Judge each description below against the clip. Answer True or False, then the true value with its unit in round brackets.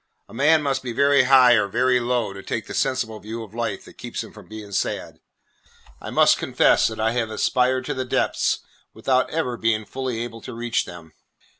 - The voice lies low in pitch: True (120 Hz)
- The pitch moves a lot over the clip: False (2.7 semitones)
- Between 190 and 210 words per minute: True (205 wpm)